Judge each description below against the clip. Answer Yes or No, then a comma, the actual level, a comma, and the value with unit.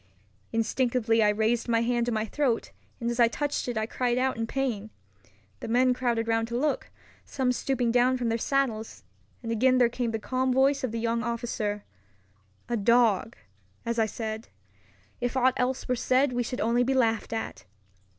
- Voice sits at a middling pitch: No, high, 235 Hz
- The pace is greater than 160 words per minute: Yes, average, 190 wpm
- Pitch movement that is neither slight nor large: No, narrow, 2.0 semitones